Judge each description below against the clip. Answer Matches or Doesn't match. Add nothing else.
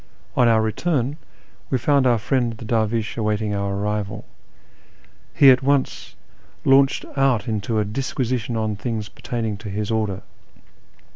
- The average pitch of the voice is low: Matches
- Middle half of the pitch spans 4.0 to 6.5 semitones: Doesn't match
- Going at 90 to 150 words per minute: Matches